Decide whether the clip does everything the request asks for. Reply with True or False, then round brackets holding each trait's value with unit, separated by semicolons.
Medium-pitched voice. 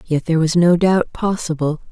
True (165 Hz)